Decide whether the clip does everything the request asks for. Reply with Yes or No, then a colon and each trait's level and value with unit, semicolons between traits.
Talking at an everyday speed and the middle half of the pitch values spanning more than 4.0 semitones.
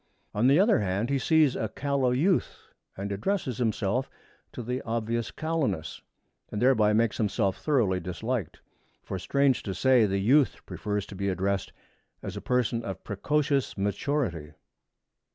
Yes: average, 150 wpm; average, 5.3 semitones